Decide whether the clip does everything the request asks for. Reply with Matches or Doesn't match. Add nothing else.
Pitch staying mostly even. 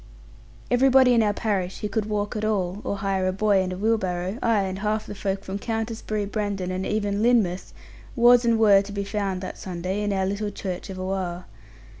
Matches